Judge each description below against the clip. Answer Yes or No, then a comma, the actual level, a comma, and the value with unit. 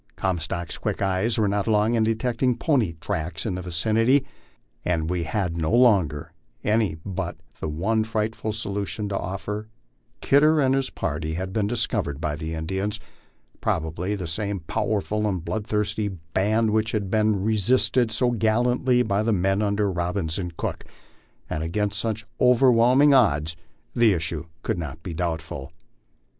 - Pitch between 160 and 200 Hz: No, low, 100 Hz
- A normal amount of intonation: Yes, average, 4.6 semitones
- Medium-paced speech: Yes, average, 155 wpm